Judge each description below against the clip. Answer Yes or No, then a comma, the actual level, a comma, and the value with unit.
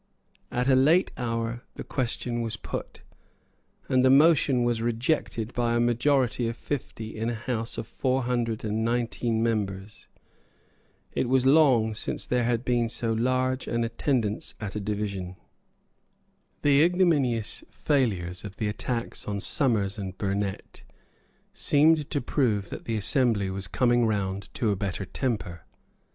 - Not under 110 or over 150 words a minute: Yes, average, 145 wpm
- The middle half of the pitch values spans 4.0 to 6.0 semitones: No, average, 3.4 semitones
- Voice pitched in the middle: No, low, 115 Hz